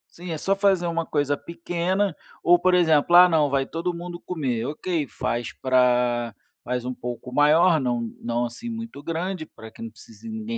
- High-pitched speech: No, medium, 155 Hz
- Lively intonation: Yes, wide, 6.1 semitones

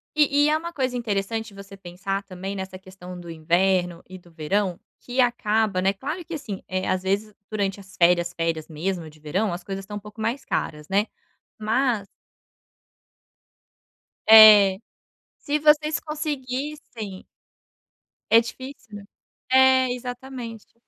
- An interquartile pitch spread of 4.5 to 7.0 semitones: Yes, average, 5.3 semitones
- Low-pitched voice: No, high, 205 Hz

